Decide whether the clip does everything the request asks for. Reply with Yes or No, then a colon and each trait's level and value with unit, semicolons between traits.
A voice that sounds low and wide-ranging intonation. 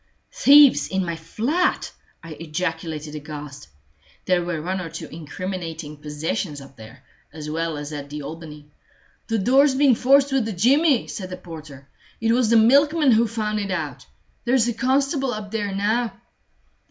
No: medium, 185 Hz; wide, 7.7 semitones